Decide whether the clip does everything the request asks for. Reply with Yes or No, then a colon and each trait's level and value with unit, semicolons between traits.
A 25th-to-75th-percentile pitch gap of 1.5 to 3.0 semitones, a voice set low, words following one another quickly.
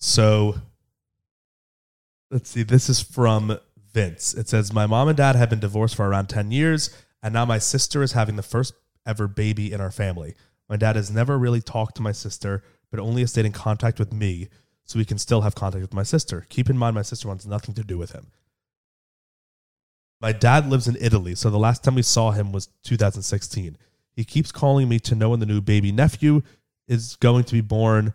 Yes: average, 2.7 semitones; low, 110 Hz; fast, 215 wpm